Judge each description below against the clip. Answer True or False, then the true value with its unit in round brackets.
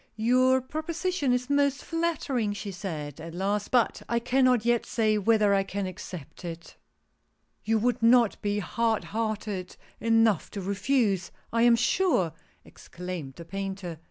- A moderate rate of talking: True (155 wpm)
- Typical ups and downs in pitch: True (4.5 semitones)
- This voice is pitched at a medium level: False (215 Hz)